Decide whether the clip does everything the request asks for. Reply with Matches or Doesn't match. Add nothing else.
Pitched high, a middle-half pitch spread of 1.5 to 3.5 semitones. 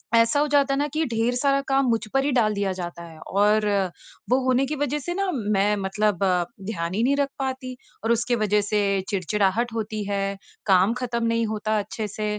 Doesn't match